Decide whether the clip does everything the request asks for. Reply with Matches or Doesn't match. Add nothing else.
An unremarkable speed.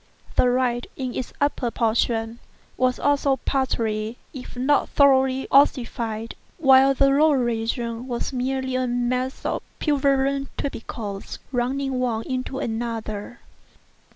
Doesn't match